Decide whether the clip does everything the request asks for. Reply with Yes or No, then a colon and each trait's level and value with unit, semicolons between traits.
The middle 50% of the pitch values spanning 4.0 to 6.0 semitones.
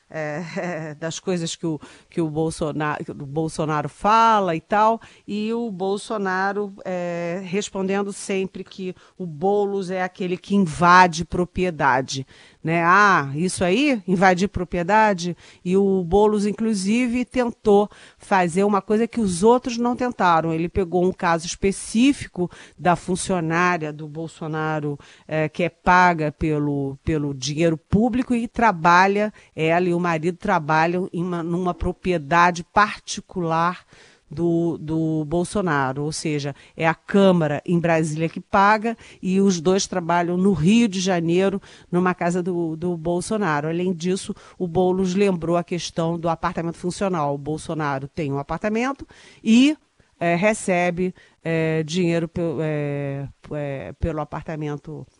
No: average, 3.4 semitones